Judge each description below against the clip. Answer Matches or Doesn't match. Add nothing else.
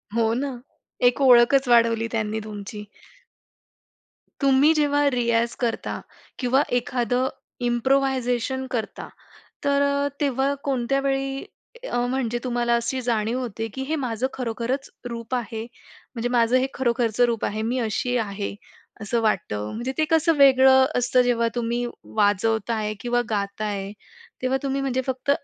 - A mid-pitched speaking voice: Doesn't match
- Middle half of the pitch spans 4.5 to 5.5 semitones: Doesn't match